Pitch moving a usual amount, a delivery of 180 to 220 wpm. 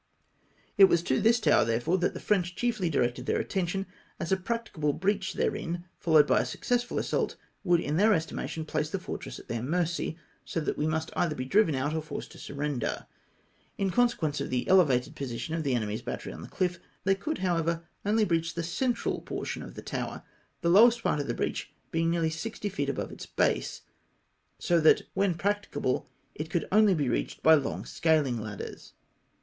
Yes: average, 4.5 semitones; average, 200 wpm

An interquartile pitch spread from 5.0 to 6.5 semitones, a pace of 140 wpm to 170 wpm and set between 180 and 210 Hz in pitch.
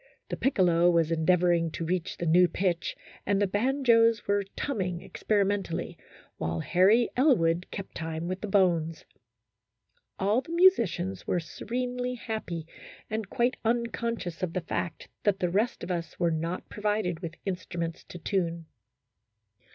No: average, 4.5 semitones; average, 150 wpm; medium, 185 Hz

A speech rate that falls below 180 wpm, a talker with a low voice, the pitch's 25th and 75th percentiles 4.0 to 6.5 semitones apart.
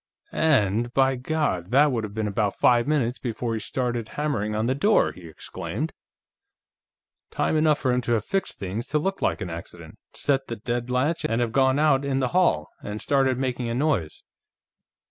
No: average, 185 wpm; low, 125 Hz; average, 4.4 semitones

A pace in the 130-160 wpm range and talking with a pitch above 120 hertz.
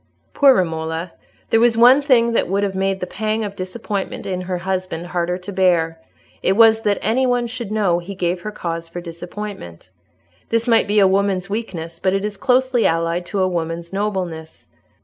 No: average, 190 wpm; high, 190 Hz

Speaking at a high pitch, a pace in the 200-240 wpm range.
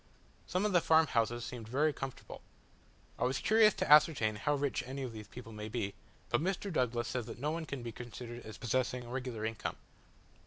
No: low, 125 Hz; fast, 205 wpm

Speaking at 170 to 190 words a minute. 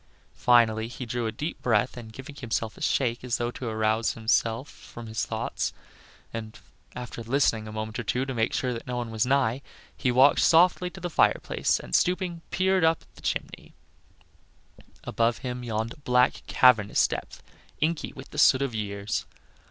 Yes: average, 180 wpm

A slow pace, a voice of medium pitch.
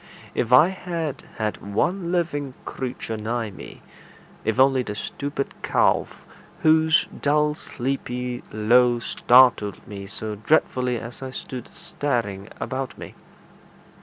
No: slow, 120 wpm; low, 125 Hz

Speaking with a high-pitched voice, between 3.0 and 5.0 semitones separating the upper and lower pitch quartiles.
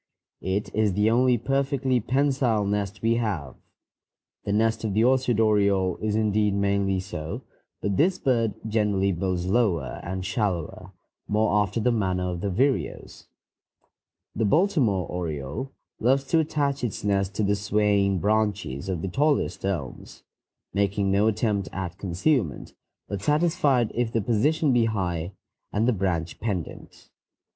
No: low, 105 Hz; average, 4.0 semitones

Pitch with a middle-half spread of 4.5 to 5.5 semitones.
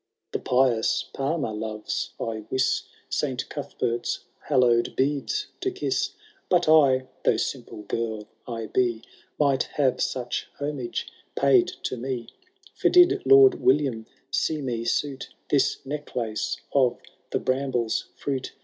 No: average, 3.8 semitones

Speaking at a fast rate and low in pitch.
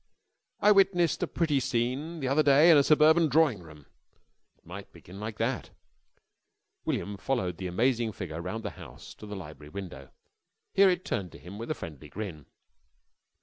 No: average, 180 wpm; low, 115 Hz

